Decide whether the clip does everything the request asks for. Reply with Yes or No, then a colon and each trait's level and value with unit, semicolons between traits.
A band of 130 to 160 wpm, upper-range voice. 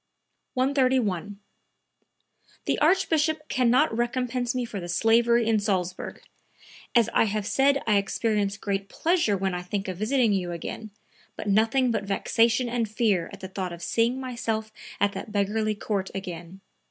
Yes: average, 155 wpm; high, 220 Hz